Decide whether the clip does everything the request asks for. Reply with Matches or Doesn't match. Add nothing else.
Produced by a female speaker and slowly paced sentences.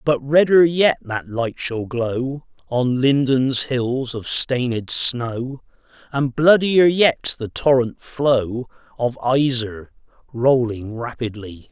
Doesn't match